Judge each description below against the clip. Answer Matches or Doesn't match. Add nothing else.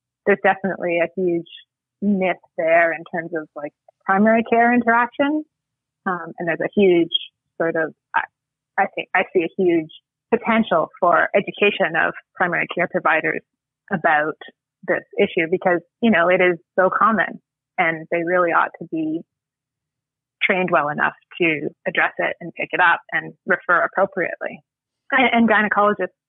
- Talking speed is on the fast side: Doesn't match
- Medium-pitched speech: Matches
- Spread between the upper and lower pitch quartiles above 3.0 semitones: Matches